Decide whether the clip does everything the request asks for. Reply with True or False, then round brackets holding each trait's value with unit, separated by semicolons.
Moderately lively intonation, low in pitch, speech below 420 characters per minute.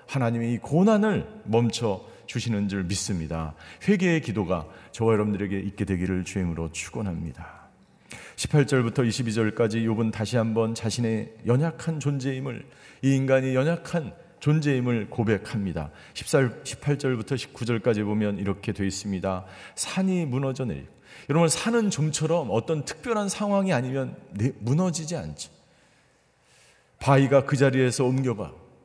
False (5.7 semitones; 120 Hz; 300 characters per minute)